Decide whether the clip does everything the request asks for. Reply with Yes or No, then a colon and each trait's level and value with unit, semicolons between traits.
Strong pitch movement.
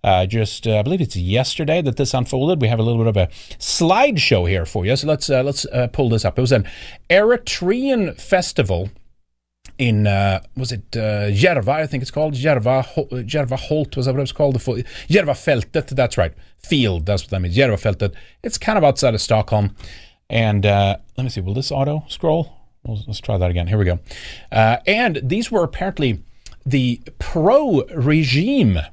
Yes: wide, 5.7 semitones